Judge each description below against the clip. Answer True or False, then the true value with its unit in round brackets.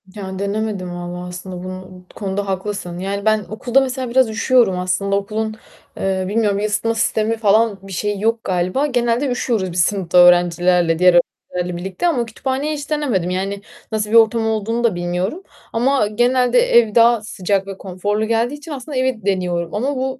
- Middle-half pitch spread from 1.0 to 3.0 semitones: False (4.2 semitones)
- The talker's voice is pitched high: True (210 Hz)